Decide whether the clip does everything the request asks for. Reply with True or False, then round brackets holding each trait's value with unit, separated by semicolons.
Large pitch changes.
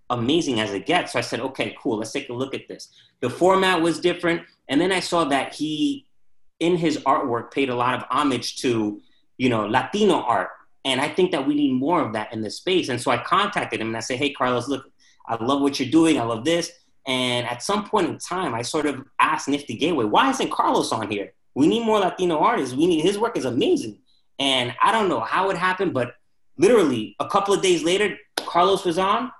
True (7.2 semitones)